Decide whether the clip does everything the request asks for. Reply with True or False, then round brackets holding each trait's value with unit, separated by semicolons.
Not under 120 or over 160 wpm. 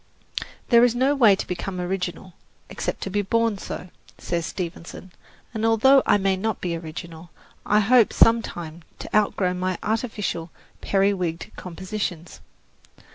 True (135 wpm)